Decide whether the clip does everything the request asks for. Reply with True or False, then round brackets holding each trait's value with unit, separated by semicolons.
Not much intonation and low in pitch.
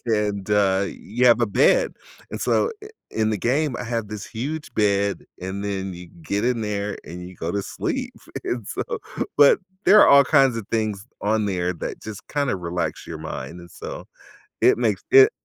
False (4.0 semitones; 105 Hz)